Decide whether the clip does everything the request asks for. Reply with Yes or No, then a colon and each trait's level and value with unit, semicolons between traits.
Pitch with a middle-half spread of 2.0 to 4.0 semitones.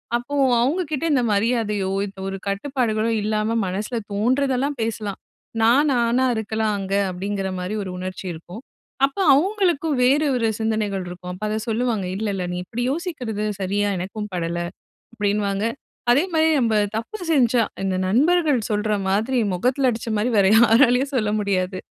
No: average, 4.5 semitones